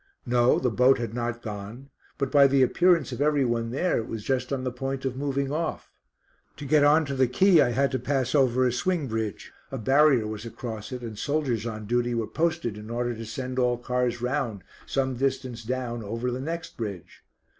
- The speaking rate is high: Yes, fast, 210 wpm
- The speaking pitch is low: Yes, low, 125 Hz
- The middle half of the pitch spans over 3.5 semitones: No, average, 2.8 semitones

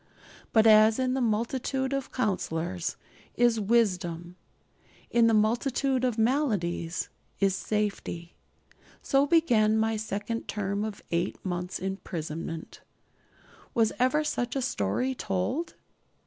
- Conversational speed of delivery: No, slow, 115 wpm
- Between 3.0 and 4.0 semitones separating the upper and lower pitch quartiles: No, average, 5.1 semitones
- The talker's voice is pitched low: No, high, 220 Hz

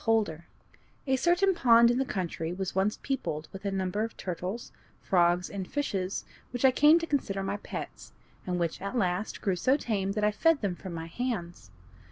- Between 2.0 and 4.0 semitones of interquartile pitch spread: No, wide, 5.4 semitones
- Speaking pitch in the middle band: No, high, 200 Hz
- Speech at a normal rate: Yes, average, 195 wpm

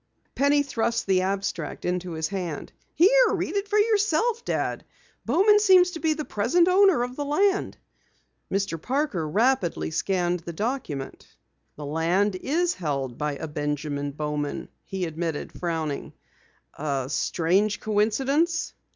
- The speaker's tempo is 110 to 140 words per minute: Yes, slow, 135 wpm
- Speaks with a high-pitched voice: Yes, high, 200 Hz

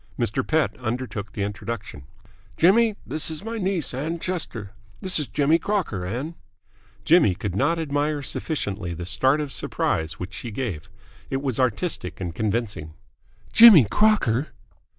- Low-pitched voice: Yes, low, 130 Hz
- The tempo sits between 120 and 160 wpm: Yes, average, 145 wpm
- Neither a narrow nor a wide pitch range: No, wide, 8.2 semitones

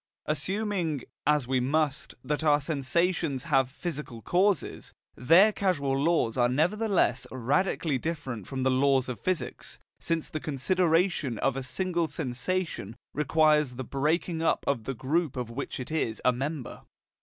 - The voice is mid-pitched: Yes, medium, 150 Hz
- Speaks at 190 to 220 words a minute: No, average, 145 wpm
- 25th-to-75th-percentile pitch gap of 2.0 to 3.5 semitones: No, average, 4.4 semitones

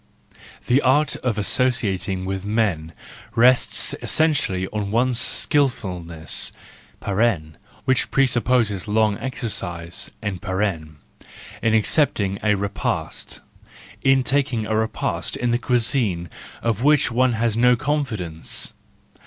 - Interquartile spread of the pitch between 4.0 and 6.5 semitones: Yes, average, 4.7 semitones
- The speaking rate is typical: No, slow, 100 wpm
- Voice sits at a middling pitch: No, low, 110 Hz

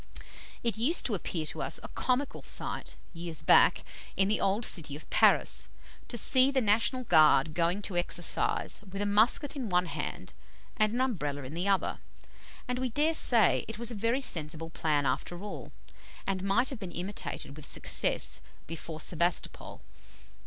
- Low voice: No, high, 195 Hz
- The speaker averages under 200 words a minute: Yes, average, 170 wpm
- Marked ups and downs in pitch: Yes, wide, 6.2 semitones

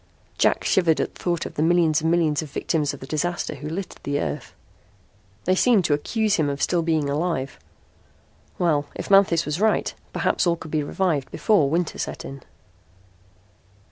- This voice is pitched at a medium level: Yes, medium, 160 Hz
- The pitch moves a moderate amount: Yes, average, 3.1 semitones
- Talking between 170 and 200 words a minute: Yes, average, 180 wpm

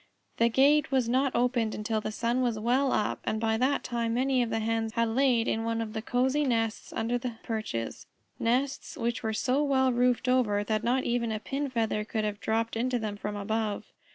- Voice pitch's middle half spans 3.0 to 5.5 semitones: No, narrow, 2.4 semitones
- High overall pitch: Yes, high, 230 Hz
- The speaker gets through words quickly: Yes, fast, 210 wpm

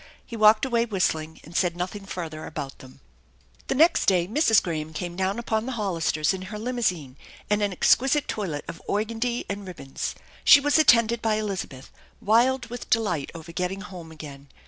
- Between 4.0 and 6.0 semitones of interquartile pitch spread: Yes, wide, 5.6 semitones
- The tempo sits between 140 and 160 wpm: No, average, 175 wpm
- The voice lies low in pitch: No, high, 195 Hz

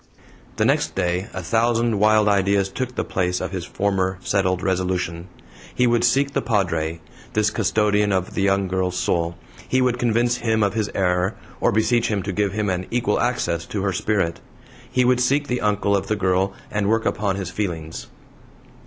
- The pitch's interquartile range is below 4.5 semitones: Yes, average, 3.3 semitones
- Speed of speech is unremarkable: Yes, average, 190 wpm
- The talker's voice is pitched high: No, low, 100 Hz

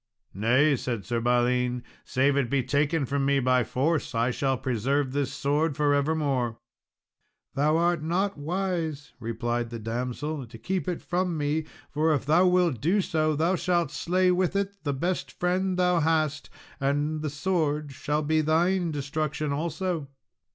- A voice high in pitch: No, medium, 150 Hz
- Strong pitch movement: No, average, 4.0 semitones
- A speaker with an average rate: Yes, average, 160 wpm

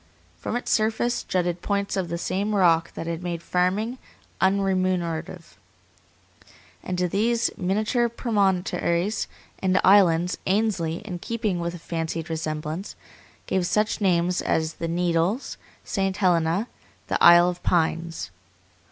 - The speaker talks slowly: Yes, slow, 125 wpm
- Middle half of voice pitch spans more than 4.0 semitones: No, average, 3.0 semitones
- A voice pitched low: No, medium, 180 Hz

